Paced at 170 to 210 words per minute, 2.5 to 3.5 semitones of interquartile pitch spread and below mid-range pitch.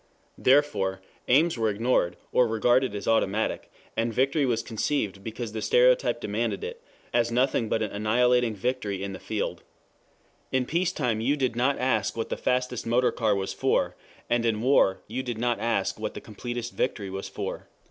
Yes: average, 180 wpm; average, 2.9 semitones; low, 120 Hz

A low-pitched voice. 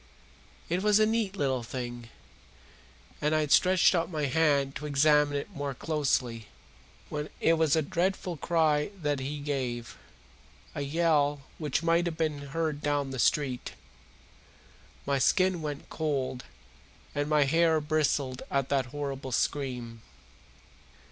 No: medium, 145 Hz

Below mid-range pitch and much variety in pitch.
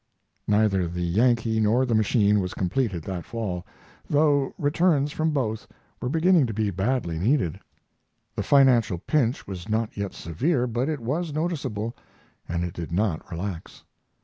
Yes: low, 110 Hz; wide, 6.4 semitones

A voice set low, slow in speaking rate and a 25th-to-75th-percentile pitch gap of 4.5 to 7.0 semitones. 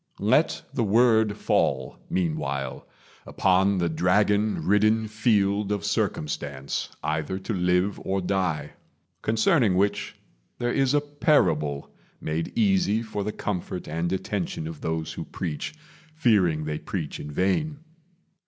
Yes: very low, 95 Hz; slow, 125 wpm; average, 5.2 semitones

